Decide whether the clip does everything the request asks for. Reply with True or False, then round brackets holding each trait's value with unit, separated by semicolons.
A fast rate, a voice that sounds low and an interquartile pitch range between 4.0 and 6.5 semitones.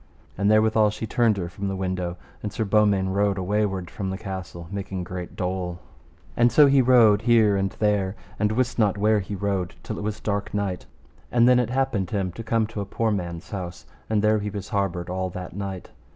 False (210 wpm; 100 Hz; 2.5 semitones)